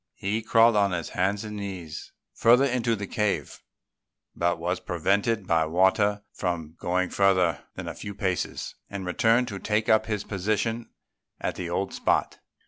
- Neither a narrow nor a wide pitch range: Yes, average, 3.4 semitones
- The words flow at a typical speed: Yes, average, 160 wpm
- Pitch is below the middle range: Yes, low, 100 Hz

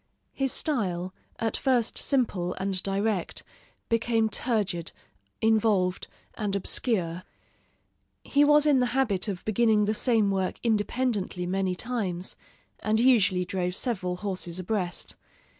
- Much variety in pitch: No, average, 4.2 semitones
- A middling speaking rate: No, slow, 120 wpm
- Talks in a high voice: Yes, high, 210 Hz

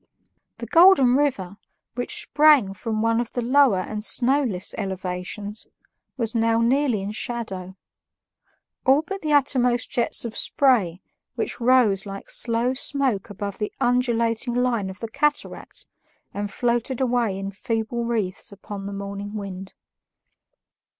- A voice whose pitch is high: Yes, high, 230 Hz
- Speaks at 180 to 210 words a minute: No, slow, 135 wpm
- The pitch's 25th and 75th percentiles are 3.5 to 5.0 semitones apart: Yes, average, 4.0 semitones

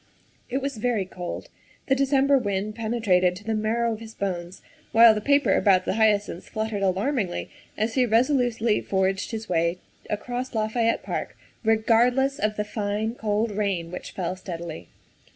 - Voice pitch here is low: No, high, 215 Hz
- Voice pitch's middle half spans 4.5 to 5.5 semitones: No, average, 3.4 semitones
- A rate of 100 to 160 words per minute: Yes, average, 155 wpm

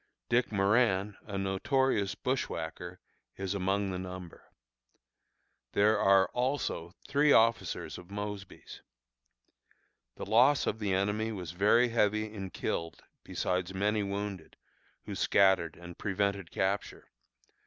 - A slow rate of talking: Yes, slow, 115 wpm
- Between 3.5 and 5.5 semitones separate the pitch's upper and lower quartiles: No, narrow, 2.5 semitones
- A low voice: Yes, low, 100 Hz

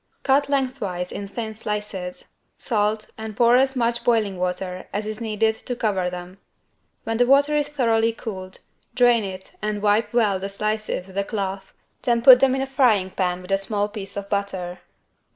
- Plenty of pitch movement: No, average, 3.5 semitones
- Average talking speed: Yes, average, 185 wpm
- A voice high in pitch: Yes, high, 215 Hz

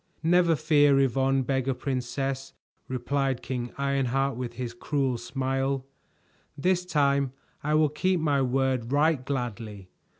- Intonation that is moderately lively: No, narrow, 2.1 semitones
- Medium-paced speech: No, slow, 125 wpm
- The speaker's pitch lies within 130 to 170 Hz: Yes, low, 135 Hz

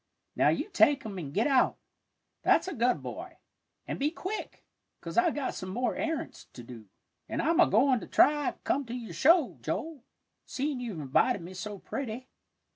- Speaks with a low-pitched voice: No, very high, 255 Hz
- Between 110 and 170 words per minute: No, average, 190 wpm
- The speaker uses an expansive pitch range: Yes, wide, 6.4 semitones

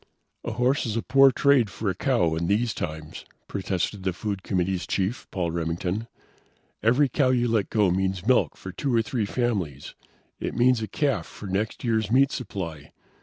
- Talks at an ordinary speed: Yes, average, 180 wpm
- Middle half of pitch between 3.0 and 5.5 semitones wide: Yes, average, 4.8 semitones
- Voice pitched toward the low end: Yes, low, 105 Hz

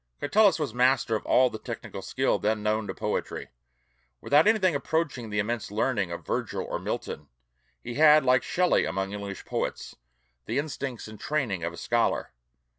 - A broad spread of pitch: Yes, wide, 5.7 semitones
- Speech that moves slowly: No, average, 170 wpm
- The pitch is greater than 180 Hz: No, low, 120 Hz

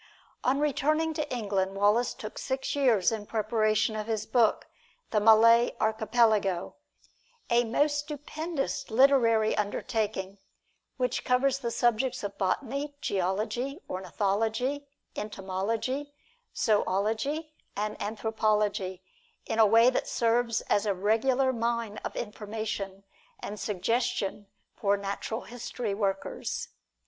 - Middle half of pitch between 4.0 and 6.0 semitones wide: No, average, 3.6 semitones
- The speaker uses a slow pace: Yes, slow, 110 wpm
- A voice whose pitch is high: Yes, high, 225 Hz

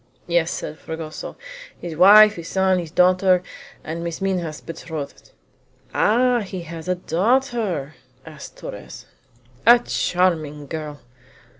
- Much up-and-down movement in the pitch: No, average, 3.2 semitones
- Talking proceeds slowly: Yes, slow, 120 wpm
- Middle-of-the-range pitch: Yes, medium, 175 Hz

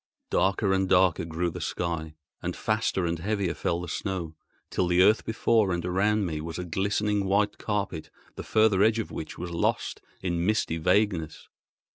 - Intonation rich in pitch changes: No, average, 3.4 semitones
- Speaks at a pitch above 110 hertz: No, very low, 95 Hz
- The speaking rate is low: No, average, 175 wpm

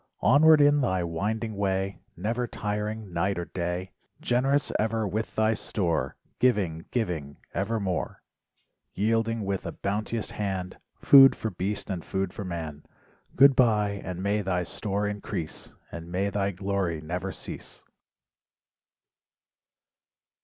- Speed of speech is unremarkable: No, slow, 125 wpm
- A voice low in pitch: Yes, low, 100 Hz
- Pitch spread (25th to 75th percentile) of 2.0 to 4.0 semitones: Yes, average, 3.5 semitones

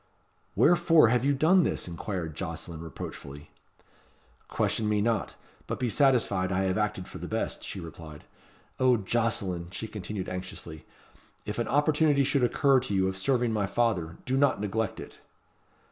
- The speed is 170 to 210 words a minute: No, average, 160 wpm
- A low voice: Yes, low, 105 Hz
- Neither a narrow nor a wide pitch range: No, wide, 5.7 semitones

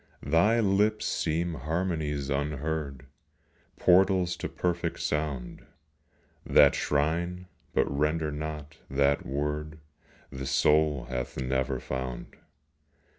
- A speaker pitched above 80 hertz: No, very low, 75 Hz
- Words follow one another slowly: Yes, slow, 95 wpm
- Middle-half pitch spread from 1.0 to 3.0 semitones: No, average, 3.4 semitones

